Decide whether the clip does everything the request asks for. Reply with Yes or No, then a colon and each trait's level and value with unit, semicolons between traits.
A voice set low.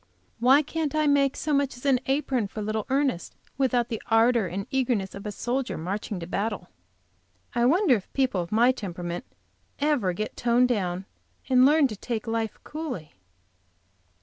No: high, 240 Hz